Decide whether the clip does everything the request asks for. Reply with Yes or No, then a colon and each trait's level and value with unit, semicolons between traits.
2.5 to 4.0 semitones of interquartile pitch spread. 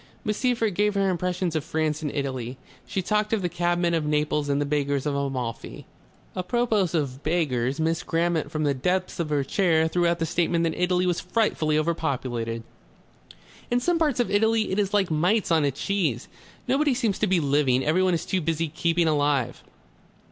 No: average, 4.5 semitones